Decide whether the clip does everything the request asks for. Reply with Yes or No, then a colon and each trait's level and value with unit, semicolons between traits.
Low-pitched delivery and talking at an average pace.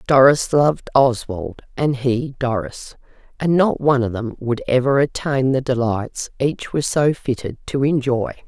Yes: low, 130 Hz; average, 155 wpm